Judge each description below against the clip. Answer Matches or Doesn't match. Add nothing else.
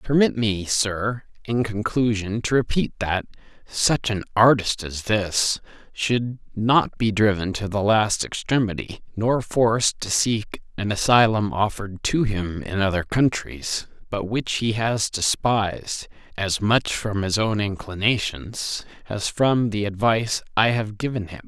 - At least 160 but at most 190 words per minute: Doesn't match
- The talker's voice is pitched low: Matches